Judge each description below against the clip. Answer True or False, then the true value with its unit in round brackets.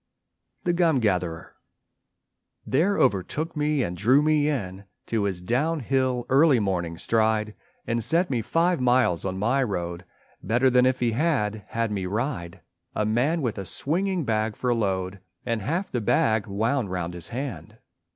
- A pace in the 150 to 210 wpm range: True (160 wpm)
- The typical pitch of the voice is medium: False (115 Hz)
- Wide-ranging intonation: True (5.9 semitones)